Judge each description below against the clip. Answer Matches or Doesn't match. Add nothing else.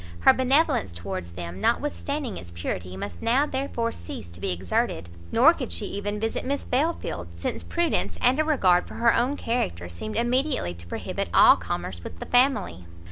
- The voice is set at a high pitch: Doesn't match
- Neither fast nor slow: Matches